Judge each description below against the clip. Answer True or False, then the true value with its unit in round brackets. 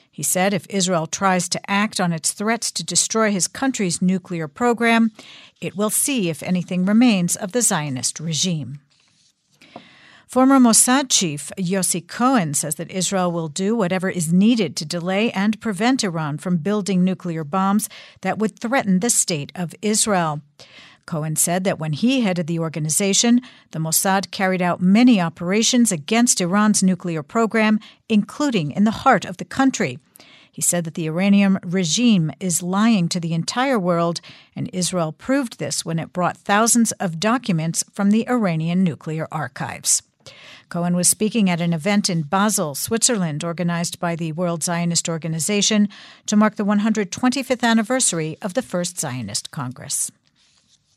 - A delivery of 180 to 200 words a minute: False (155 wpm)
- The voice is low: False (185 Hz)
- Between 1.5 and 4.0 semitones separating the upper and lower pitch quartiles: False (4.4 semitones)